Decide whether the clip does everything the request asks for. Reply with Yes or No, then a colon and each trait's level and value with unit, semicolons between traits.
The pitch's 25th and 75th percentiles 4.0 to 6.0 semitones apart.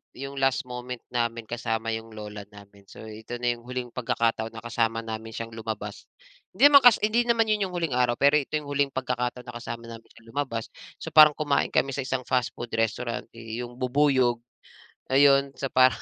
No: average, 3.3 semitones